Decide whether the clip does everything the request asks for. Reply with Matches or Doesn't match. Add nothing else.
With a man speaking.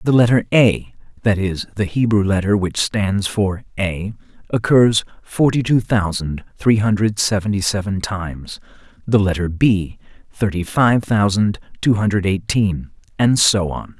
Matches